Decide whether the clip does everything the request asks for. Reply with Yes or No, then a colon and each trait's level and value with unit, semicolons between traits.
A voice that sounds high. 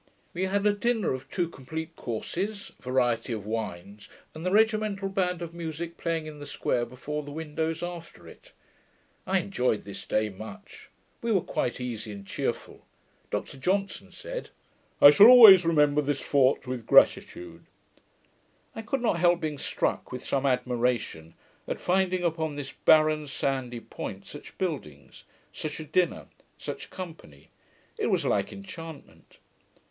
No: medium, 155 Hz